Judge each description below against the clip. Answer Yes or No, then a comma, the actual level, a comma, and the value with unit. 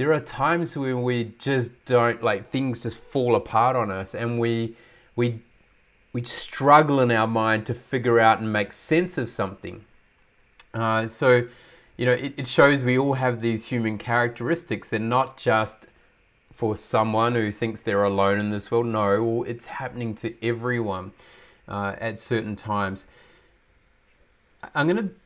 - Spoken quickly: No, average, 155 wpm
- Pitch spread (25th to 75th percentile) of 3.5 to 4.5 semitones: No, average, 2.7 semitones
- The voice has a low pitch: Yes, low, 115 Hz